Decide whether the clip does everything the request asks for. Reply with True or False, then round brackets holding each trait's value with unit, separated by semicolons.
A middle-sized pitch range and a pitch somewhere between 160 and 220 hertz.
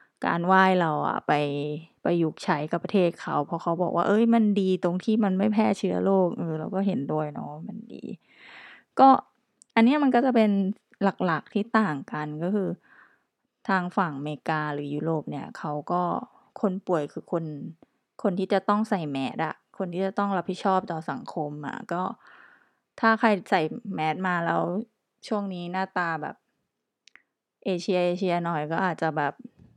True (4.1 semitones; 185 Hz)